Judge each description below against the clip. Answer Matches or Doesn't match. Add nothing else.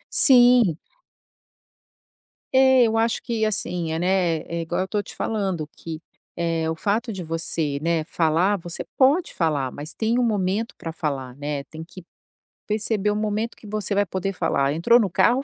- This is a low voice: Doesn't match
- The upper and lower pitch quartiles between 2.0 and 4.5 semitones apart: Doesn't match